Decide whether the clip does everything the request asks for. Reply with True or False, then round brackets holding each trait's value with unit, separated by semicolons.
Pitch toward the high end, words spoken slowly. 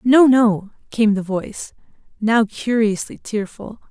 True (220 Hz; 125 wpm)